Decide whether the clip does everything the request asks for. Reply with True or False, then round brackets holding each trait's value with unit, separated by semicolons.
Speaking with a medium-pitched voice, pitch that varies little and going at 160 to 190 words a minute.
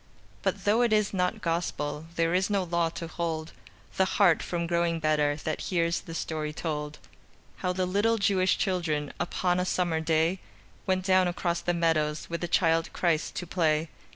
True (170 Hz; 2.3 semitones; 180 wpm)